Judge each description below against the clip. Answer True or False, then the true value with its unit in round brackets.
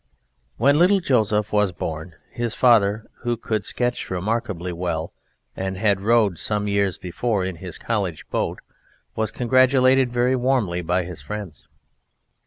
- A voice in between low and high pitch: False (105 Hz)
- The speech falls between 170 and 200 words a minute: False (140 wpm)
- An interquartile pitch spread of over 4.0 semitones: True (4.8 semitones)